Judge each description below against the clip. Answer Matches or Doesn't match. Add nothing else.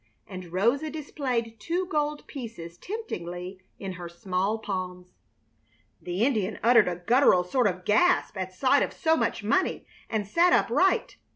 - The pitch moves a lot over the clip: Matches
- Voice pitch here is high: Matches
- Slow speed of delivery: Doesn't match